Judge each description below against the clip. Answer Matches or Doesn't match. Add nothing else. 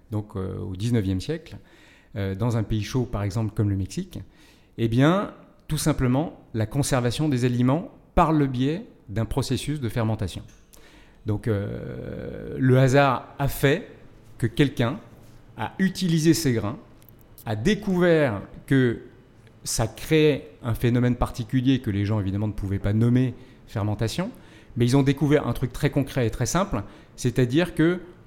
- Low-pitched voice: Matches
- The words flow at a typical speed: Matches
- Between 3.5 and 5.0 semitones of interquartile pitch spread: Matches